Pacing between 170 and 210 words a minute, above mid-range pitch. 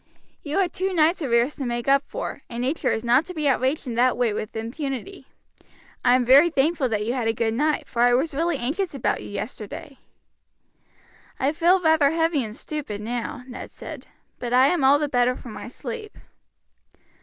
Yes: average, 200 wpm; very high, 265 Hz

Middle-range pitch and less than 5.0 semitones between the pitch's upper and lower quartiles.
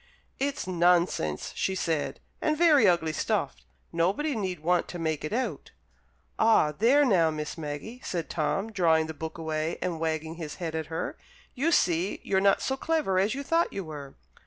No: medium, 175 Hz; wide, 5.5 semitones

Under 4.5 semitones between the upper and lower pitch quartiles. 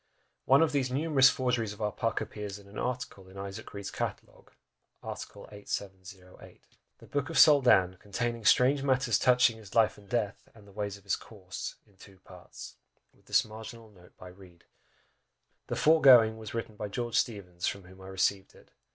Yes: average, 4.1 semitones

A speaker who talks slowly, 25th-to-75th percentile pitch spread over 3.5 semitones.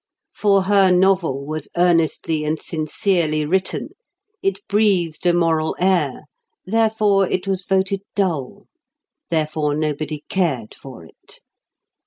Yes: slow, 115 wpm; average, 3.9 semitones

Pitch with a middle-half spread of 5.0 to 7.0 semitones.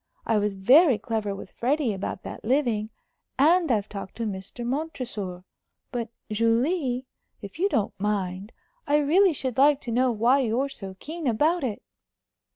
Yes: average, 5.3 semitones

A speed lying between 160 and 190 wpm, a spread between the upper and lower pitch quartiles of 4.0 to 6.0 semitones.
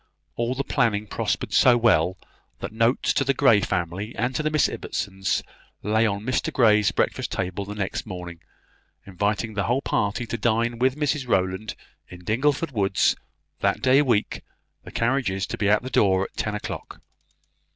Yes: average, 170 wpm; average, 4.3 semitones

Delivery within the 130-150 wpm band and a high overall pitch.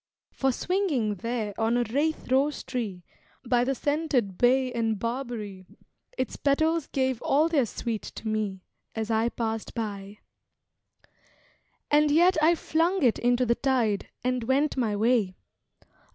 Yes: average, 140 wpm; high, 245 Hz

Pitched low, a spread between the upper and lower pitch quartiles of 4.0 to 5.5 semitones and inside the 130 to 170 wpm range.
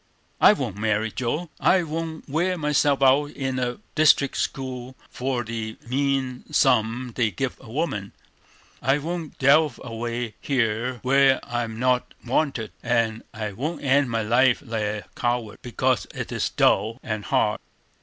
No: low, 125 Hz; average, 3.5 semitones; average, 150 wpm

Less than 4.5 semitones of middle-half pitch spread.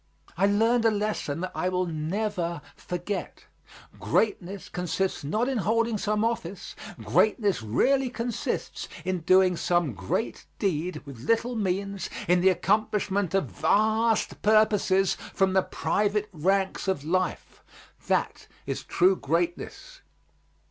Yes: average, 3.3 semitones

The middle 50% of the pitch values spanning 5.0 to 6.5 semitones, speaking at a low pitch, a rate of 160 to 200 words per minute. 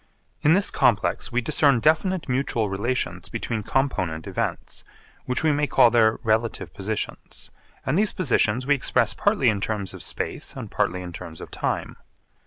Yes: wide, 5.6 semitones; low, 115 Hz; average, 165 wpm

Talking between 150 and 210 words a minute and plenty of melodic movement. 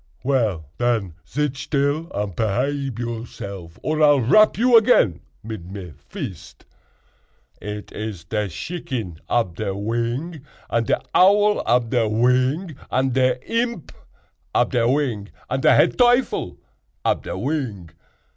No: slow, 135 wpm; wide, 5.9 semitones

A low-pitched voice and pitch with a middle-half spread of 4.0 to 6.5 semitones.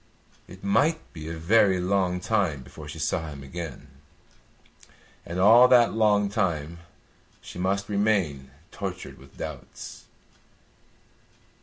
Yes: very low, 90 Hz; average, 4.6 semitones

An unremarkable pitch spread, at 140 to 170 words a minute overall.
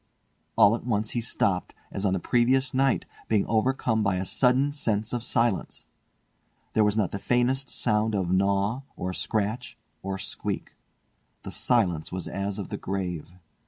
Yes: average, 3.9 semitones; average, 160 wpm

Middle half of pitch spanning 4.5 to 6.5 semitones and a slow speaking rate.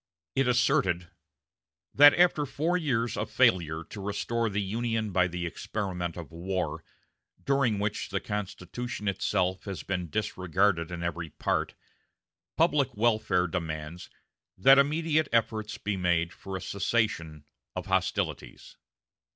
Yes: average, 5.1 semitones; slow, 125 wpm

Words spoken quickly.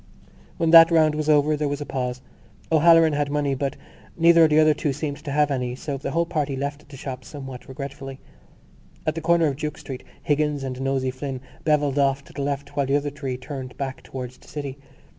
Yes: fast, 215 wpm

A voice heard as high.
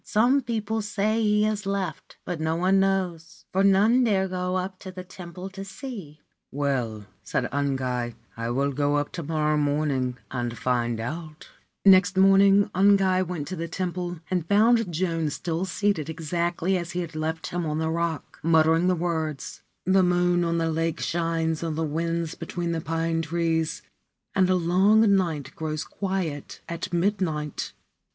No: medium, 170 Hz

